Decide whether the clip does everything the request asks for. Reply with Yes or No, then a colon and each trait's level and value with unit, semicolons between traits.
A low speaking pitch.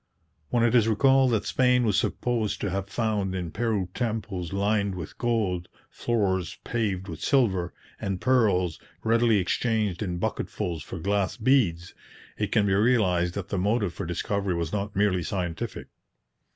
Yes: low, 100 Hz